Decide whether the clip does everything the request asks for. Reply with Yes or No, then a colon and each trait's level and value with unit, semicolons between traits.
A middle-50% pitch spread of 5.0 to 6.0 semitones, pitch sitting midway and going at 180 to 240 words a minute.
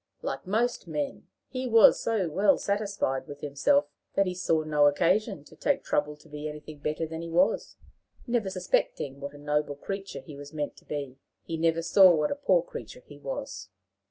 Yes: average, 5.3 semitones; medium, 165 Hz; average, 190 wpm